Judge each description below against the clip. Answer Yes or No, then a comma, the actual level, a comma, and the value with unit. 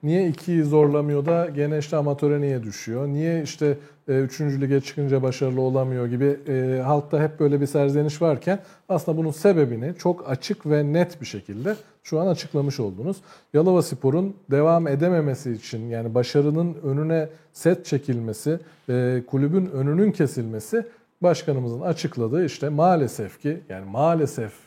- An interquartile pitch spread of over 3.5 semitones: Yes, average, 4.0 semitones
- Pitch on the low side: No, medium, 150 Hz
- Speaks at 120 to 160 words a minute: Yes, fast, 140 wpm